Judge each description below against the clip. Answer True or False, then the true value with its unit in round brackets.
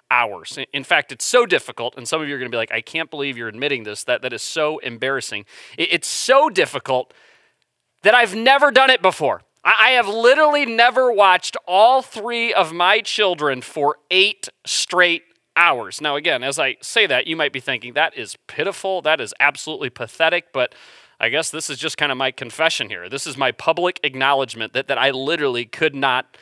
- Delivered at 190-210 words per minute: True (200 wpm)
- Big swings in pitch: True (6.6 semitones)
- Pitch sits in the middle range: True (155 Hz)